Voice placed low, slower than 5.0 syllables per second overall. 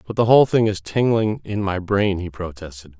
No: low, 100 Hz; 5.4 syllables/s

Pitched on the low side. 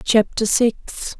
No: high, 225 Hz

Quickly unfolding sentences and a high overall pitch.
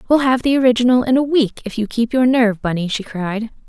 Yes: fast, 245 wpm; high, 235 Hz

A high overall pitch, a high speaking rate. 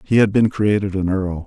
No: low, 100 Hz; fast, 245 wpm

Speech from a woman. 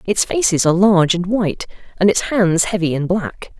Yes: female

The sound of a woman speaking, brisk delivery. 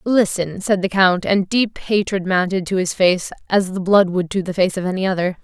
Yes: female; fast, 230 wpm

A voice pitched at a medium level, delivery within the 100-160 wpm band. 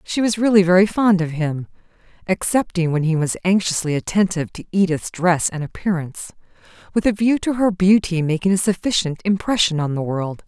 No: medium, 180 Hz; average, 180 wpm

